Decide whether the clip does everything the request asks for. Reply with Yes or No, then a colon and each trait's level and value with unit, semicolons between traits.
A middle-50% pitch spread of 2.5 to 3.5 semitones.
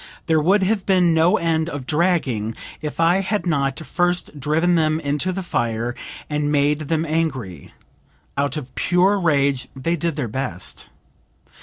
No: average, 3.9 semitones